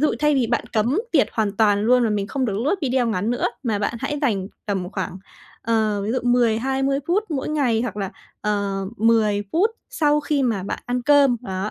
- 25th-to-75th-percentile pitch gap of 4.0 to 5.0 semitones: Yes, average, 4.7 semitones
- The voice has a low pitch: No, high, 230 Hz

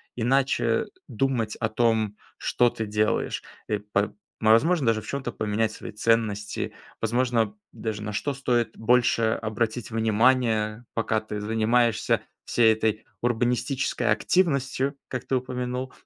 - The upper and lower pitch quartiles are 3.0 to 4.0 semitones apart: No, narrow, 2.4 semitones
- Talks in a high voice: No, low, 115 Hz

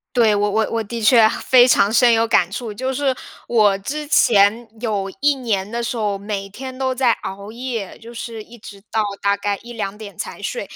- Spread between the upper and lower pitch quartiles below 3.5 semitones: Yes, average, 3.1 semitones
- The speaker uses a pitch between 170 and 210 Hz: No, high, 225 Hz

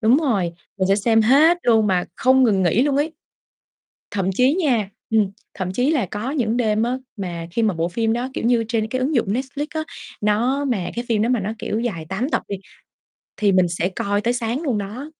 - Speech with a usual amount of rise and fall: Yes, average, 4.3 semitones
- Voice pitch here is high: Yes, high, 225 Hz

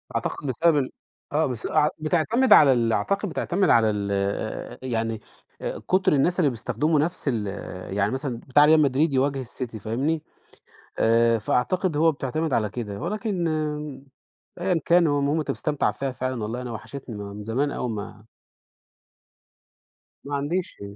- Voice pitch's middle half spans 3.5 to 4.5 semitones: No, wide, 5.5 semitones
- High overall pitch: No, medium, 140 Hz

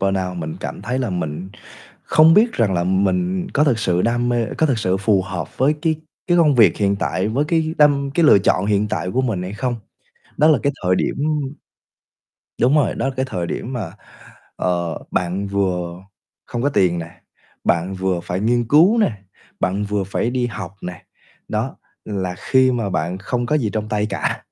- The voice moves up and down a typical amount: No, wide, 6.1 semitones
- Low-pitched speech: Yes, low, 105 Hz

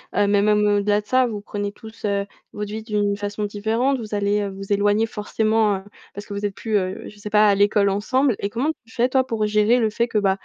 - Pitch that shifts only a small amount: Yes, narrow, 1.5 semitones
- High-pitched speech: Yes, high, 210 Hz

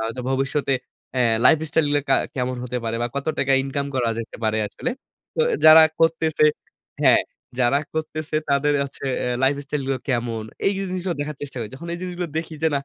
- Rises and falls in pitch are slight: No, average, 3.7 semitones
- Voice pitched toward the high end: No, medium, 140 Hz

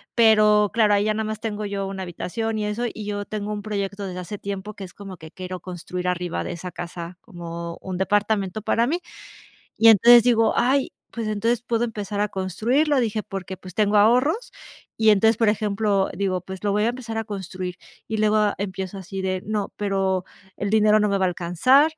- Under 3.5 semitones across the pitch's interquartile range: Yes, average, 2.7 semitones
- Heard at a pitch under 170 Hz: No, high, 205 Hz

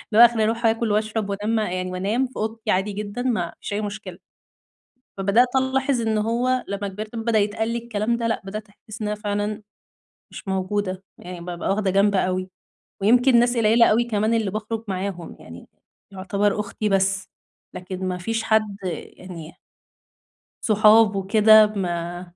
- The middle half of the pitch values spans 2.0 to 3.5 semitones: Yes, average, 2.7 semitones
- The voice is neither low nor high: No, high, 210 Hz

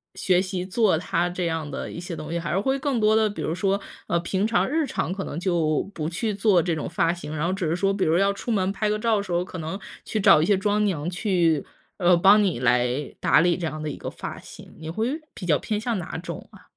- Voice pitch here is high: No, medium, 180 Hz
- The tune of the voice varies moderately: Yes, average, 3.7 semitones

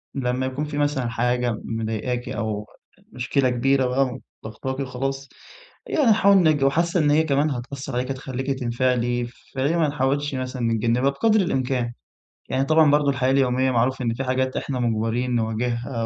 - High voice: No, low, 130 Hz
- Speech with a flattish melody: Yes, narrow, 2.2 semitones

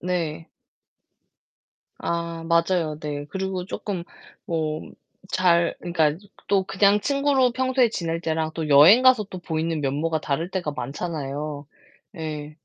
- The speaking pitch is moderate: Yes, medium, 170 Hz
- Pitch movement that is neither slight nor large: Yes, average, 3.6 semitones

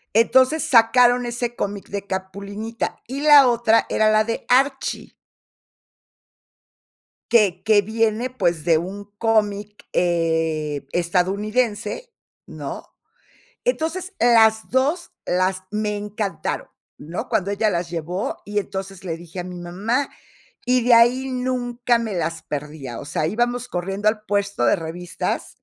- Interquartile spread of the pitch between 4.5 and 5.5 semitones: Yes, average, 5.1 semitones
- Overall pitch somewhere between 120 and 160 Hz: No, high, 210 Hz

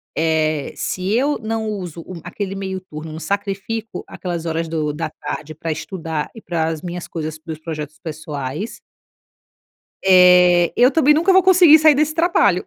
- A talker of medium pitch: Yes, medium, 180 Hz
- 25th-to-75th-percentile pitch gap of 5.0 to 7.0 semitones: Yes, average, 5.3 semitones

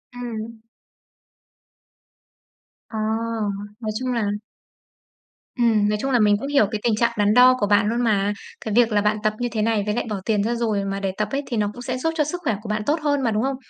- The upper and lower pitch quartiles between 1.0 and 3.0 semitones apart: Yes, average, 2.7 semitones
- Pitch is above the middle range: Yes, high, 225 Hz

